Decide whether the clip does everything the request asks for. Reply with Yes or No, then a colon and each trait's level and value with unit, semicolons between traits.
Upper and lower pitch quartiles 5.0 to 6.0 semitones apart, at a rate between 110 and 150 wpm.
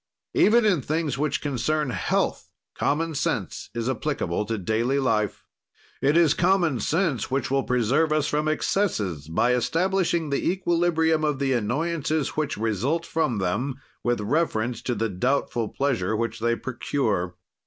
Yes: wide, 5.6 semitones; average, 145 wpm